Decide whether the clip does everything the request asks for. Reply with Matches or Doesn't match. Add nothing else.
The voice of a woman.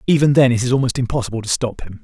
Doesn't match